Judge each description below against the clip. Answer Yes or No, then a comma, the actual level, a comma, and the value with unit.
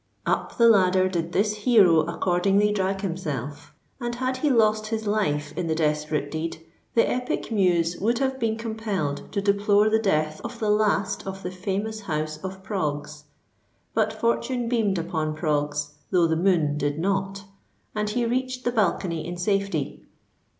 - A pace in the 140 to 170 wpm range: Yes, average, 165 wpm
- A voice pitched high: Yes, high, 195 Hz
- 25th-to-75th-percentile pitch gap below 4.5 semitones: No, average, 5.2 semitones